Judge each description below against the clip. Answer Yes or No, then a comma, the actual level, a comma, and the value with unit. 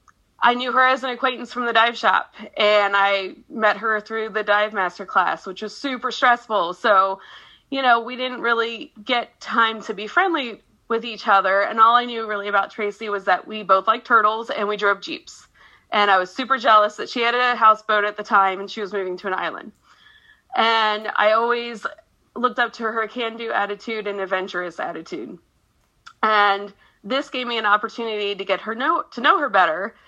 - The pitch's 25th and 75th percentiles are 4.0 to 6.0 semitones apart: No, average, 2.9 semitones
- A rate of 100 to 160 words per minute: No, average, 200 wpm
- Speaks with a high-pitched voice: Yes, high, 220 Hz